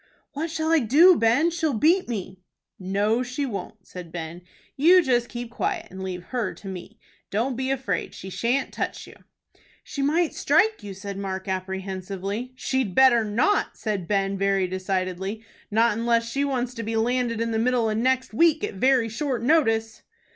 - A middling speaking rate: Yes, average, 175 wpm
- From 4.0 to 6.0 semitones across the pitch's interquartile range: Yes, average, 5.2 semitones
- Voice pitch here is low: No, high, 230 Hz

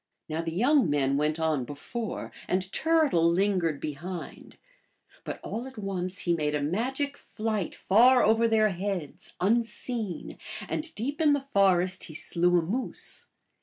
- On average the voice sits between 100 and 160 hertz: No, high, 190 Hz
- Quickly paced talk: No, average, 150 wpm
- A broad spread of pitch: Yes, wide, 6.0 semitones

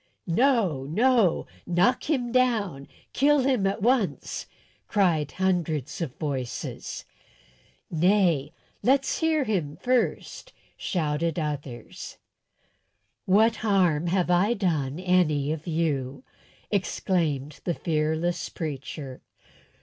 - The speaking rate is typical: No, slow, 95 wpm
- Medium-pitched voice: Yes, medium, 175 Hz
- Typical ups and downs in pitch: No, wide, 6.2 semitones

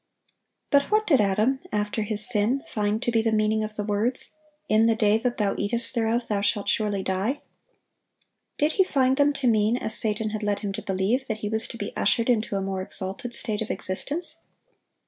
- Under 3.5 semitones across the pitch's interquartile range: Yes, average, 2.9 semitones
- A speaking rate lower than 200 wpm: No, fast, 205 wpm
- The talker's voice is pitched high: Yes, high, 220 Hz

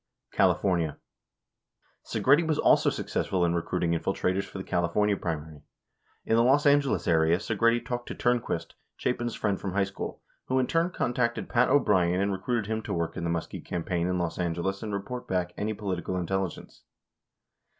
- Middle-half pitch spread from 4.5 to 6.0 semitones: Yes, wide, 5.4 semitones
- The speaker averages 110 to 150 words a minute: No, average, 170 wpm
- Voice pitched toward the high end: No, low, 100 Hz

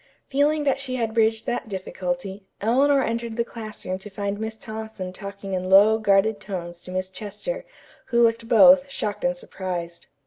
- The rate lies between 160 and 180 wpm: Yes, average, 170 wpm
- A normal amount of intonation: Yes, average, 3.7 semitones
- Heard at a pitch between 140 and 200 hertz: No, high, 220 Hz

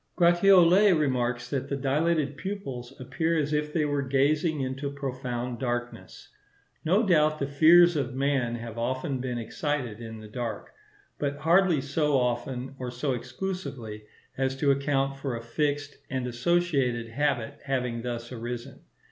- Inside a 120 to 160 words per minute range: Yes, average, 150 wpm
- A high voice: No, low, 135 Hz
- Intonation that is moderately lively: Yes, average, 3.6 semitones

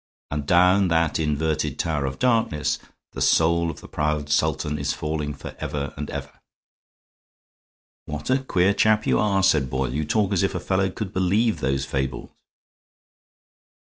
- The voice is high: No, very low, 80 Hz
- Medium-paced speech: Yes, average, 155 wpm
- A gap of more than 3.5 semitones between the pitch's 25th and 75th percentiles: Yes, average, 4.7 semitones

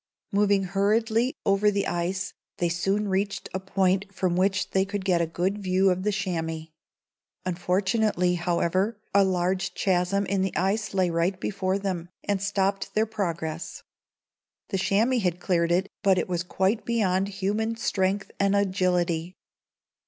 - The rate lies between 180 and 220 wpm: No, average, 150 wpm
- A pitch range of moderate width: No, narrow, 1.9 semitones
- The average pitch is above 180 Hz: Yes, high, 190 Hz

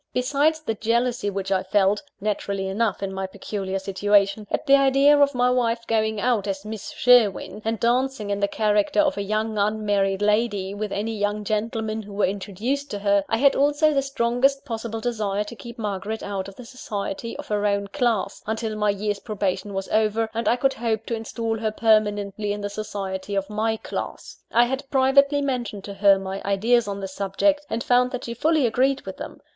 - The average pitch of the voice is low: No, high, 215 Hz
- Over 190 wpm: Yes, average, 200 wpm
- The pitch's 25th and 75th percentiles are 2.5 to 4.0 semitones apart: Yes, average, 3.2 semitones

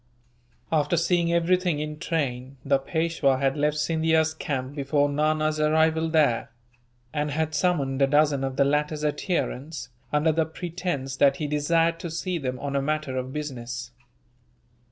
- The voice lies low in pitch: No, medium, 150 Hz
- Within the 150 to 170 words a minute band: Yes, average, 155 wpm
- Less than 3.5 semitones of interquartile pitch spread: Yes, average, 2.7 semitones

